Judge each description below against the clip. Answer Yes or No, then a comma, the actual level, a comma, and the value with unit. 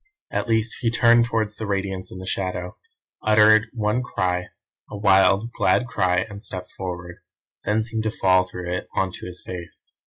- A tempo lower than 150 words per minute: No, average, 180 wpm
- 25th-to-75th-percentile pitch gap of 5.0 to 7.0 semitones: No, average, 3.1 semitones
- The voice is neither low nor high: No, low, 100 Hz